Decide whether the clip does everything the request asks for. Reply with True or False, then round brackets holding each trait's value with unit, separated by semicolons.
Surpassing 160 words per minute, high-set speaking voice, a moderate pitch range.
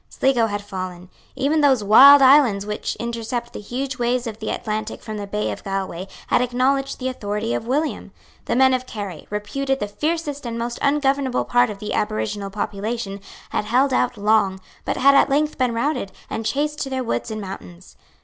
True (190 wpm; 235 Hz; 4.6 semitones)